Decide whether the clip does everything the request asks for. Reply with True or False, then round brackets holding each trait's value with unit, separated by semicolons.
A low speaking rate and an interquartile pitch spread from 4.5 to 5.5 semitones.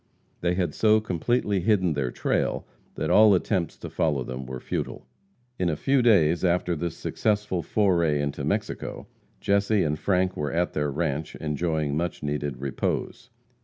False (160 wpm; 5.1 semitones)